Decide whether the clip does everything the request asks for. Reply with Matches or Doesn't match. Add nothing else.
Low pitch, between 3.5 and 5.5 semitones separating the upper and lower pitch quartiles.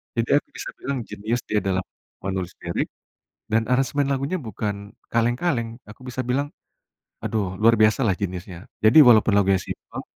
Matches